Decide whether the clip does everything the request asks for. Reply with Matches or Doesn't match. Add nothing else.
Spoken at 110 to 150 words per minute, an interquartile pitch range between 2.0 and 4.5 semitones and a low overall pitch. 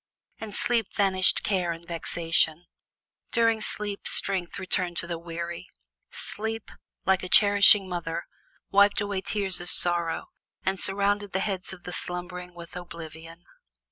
Doesn't match